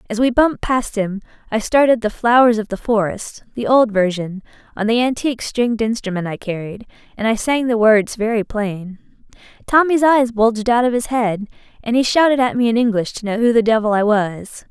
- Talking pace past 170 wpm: Yes, average, 195 wpm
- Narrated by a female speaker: Yes, female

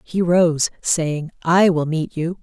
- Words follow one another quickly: No, average, 175 wpm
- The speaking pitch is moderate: Yes, medium, 165 Hz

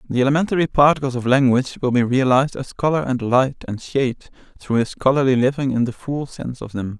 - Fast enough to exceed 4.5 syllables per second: Yes, 6.1 syllables/s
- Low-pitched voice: Yes, low, 130 Hz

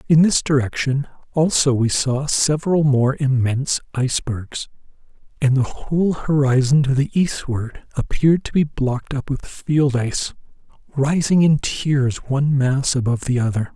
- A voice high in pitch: No, low, 135 Hz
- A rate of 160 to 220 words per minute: No, average, 145 wpm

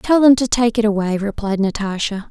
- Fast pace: Yes, fast, 210 wpm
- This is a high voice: Yes, high, 215 Hz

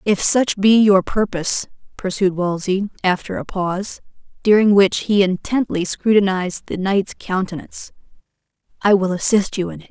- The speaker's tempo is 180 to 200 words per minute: No, average, 145 wpm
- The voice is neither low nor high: No, high, 195 Hz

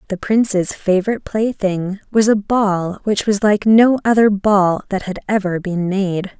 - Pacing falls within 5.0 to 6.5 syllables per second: No, 4.3 syllables/s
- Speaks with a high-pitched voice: Yes, high, 200 Hz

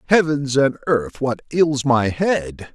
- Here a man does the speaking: Yes, male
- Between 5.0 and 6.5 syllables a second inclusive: No, 3.5 syllables/s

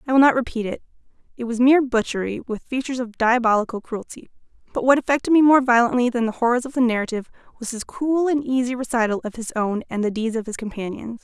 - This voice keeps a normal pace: No, fast, 220 wpm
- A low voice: No, high, 240 Hz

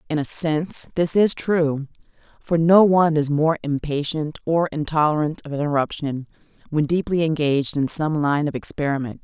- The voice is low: No, medium, 155 Hz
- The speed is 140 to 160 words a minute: Yes, average, 155 wpm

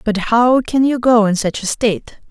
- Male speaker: No, female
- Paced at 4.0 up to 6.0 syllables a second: Yes, 4.7 syllables/s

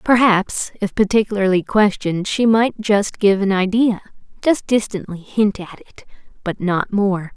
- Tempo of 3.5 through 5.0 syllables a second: Yes, 4.6 syllables/s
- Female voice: Yes, female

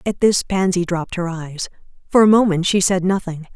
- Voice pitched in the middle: Yes, medium, 180 Hz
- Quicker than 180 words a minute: Yes, fast, 205 wpm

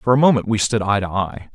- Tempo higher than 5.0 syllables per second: Yes, 6.1 syllables/s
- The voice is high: No, low, 110 Hz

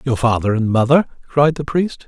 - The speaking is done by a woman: No, male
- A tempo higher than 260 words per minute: No, fast, 205 wpm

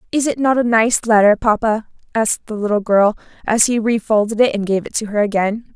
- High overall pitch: Yes, high, 220 Hz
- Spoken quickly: Yes, fast, 210 wpm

